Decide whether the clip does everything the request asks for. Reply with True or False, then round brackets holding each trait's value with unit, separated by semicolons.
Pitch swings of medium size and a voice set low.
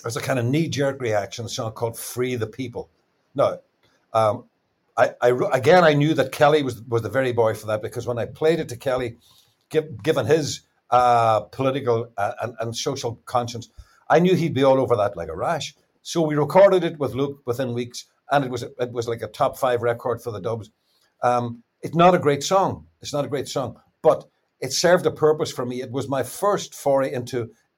True (3.7 semitones; 125 Hz)